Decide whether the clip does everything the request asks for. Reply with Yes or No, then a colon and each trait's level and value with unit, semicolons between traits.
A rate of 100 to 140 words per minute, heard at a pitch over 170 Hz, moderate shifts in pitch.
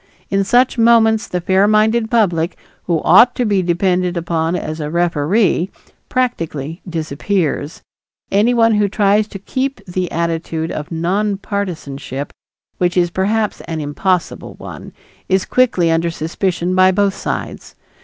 Yes: slow, 135 wpm; medium, 185 Hz; average, 4.0 semitones